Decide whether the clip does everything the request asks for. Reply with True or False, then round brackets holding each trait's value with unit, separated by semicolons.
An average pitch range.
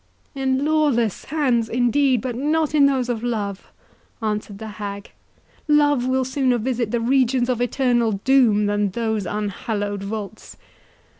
True (3.9 semitones)